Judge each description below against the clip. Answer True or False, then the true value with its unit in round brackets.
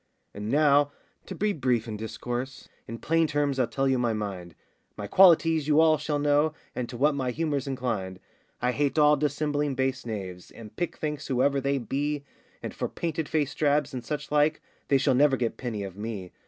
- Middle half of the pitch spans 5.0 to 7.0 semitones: False (4.1 semitones)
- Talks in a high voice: False (135 Hz)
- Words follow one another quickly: False (195 wpm)